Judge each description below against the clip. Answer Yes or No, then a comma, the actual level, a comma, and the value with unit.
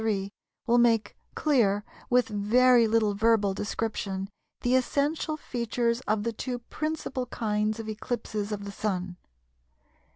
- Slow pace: Yes, slow, 130 wpm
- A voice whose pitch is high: Yes, high, 225 Hz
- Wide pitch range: No, average, 2.9 semitones